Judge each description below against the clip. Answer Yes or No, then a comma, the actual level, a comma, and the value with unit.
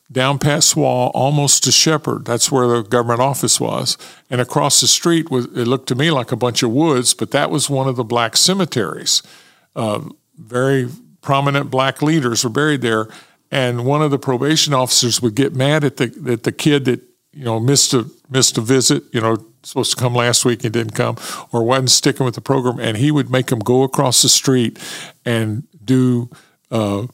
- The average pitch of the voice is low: Yes, low, 130 Hz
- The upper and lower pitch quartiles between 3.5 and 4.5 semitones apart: No, average, 2.8 semitones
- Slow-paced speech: No, fast, 205 wpm